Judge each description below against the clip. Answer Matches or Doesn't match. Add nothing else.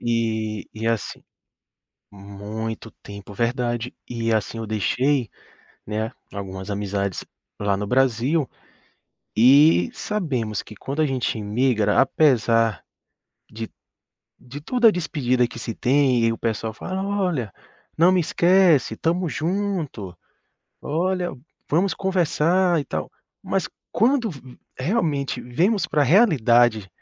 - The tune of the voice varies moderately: Doesn't match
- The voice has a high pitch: Doesn't match